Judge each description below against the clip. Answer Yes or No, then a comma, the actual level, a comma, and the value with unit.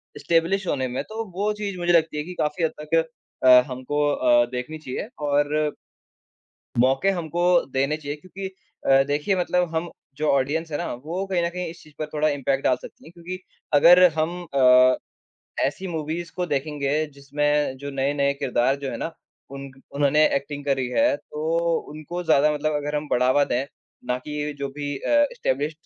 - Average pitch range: Yes, average, 3.4 semitones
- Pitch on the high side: No, medium, 150 Hz